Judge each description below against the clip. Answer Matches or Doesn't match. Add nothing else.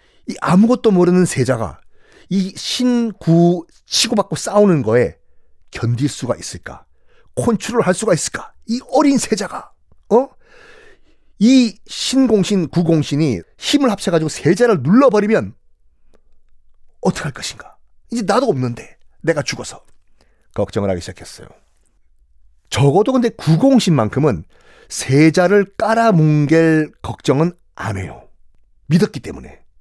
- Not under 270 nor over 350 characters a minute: Doesn't match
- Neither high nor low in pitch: Matches